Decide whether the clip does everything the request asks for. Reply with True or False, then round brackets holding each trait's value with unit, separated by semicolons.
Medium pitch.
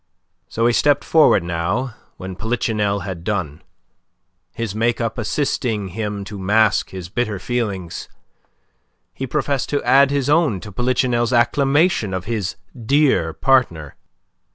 False (110 Hz)